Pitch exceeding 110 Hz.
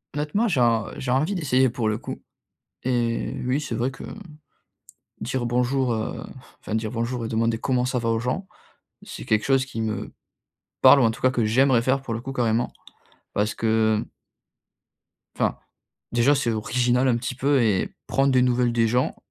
Yes: low, 125 Hz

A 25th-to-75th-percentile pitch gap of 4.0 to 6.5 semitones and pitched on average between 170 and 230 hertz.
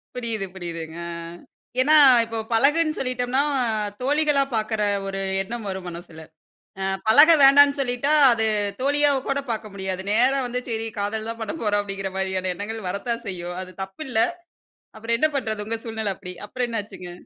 Yes: average, 4.7 semitones; high, 225 Hz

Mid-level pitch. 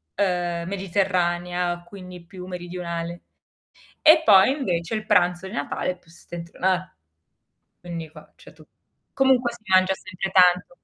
Yes: medium, 180 Hz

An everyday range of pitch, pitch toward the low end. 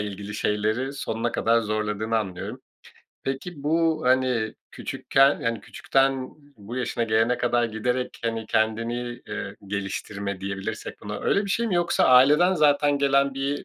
Yes: average, 4.2 semitones; low, 120 Hz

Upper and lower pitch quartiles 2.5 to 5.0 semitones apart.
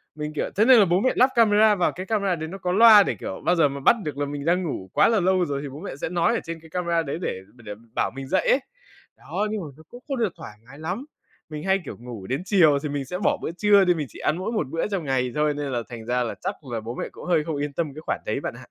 No: wide, 5.6 semitones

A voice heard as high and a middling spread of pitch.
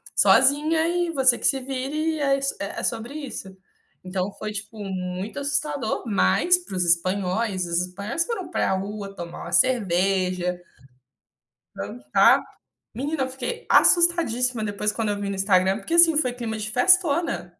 No: high, 220 Hz; wide, 7.0 semitones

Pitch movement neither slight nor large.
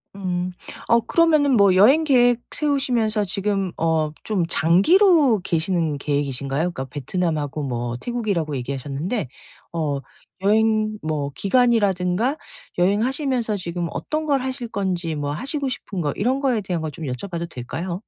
No: wide, 7.3 semitones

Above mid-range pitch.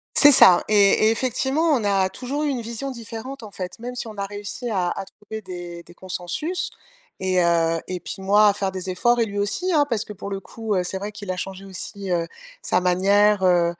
Yes: high, 200 Hz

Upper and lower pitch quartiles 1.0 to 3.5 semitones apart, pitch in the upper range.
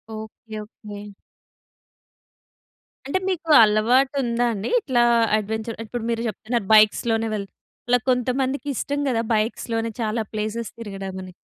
Yes: narrow, 2.5 semitones; high, 225 Hz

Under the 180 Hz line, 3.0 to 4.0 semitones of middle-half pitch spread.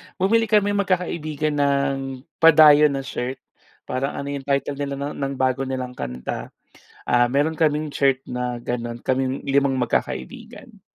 No: medium, 140 Hz; narrow, 2.6 semitones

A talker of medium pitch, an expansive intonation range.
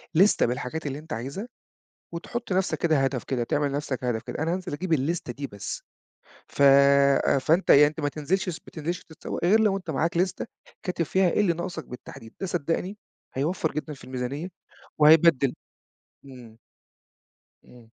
No: medium, 155 Hz; average, 4.8 semitones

